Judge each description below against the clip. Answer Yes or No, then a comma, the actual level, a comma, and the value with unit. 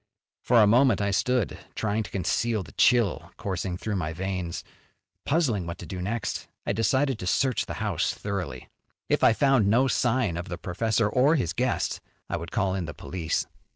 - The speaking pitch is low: Yes, low, 100 Hz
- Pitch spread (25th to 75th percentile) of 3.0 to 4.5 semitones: No, average, 5.0 semitones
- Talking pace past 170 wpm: Yes, average, 190 wpm